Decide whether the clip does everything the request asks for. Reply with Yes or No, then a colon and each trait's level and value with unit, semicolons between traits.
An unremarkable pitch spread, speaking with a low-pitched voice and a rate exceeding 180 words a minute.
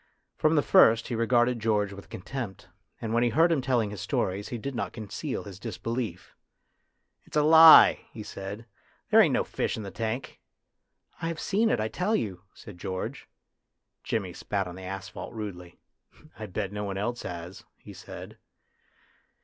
Yes: average, 4.3 semitones; low, 110 Hz; average, 190 wpm